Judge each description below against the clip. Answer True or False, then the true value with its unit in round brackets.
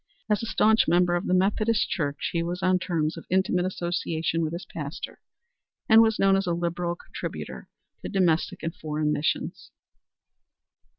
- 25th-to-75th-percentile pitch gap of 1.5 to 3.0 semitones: True (2.5 semitones)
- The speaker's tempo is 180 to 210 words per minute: False (165 wpm)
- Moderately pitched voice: True (175 Hz)